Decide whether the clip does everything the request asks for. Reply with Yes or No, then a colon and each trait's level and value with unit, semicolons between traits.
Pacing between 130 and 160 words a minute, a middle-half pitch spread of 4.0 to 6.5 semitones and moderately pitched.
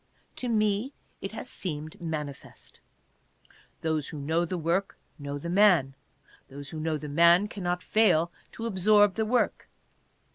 Yes: average, 145 wpm; average, 5.1 semitones; medium, 170 Hz